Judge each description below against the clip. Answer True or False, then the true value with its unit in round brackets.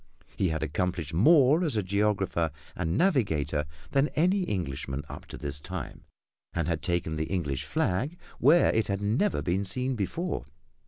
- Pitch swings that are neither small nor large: False (8.1 semitones)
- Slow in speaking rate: False (160 wpm)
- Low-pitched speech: True (95 Hz)